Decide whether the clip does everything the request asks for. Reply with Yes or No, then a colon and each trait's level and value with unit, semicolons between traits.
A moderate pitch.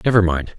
No: very low, 95 Hz